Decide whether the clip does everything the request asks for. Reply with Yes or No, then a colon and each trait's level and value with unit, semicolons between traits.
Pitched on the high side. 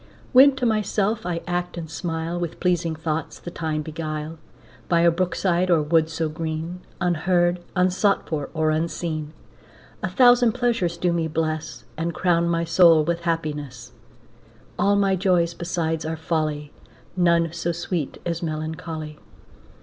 No: medium, 170 Hz